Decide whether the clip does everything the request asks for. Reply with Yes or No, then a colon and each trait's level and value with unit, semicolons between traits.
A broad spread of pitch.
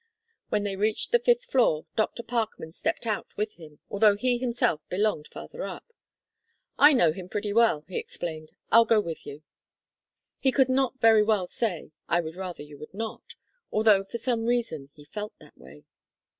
Yes: wide, 5.7 semitones